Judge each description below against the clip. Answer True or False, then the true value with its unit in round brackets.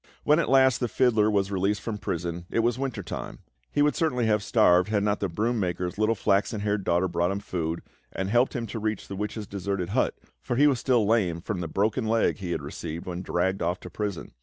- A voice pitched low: True (105 Hz)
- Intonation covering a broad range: False (4.1 semitones)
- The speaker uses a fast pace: True (235 wpm)